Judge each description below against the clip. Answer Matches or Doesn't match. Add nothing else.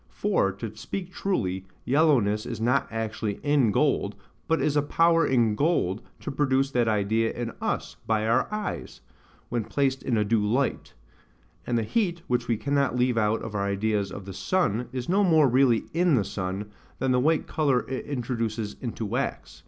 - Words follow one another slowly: Doesn't match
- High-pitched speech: Doesn't match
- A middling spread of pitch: Matches